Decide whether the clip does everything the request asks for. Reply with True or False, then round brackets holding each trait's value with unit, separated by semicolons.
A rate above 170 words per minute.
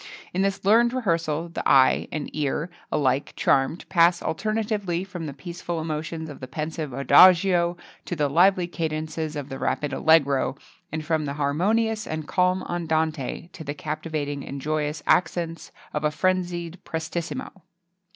False (155 wpm)